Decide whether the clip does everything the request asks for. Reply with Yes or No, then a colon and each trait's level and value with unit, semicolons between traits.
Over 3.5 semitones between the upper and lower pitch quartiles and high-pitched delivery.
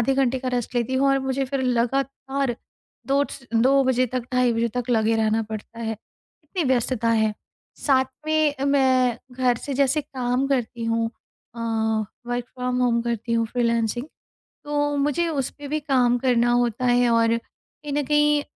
No: average, 2.9 semitones; very high, 250 Hz